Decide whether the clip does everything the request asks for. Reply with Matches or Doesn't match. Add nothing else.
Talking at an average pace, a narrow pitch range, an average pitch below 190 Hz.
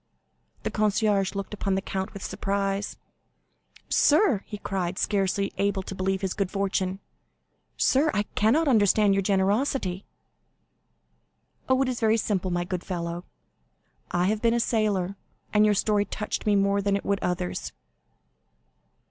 Doesn't match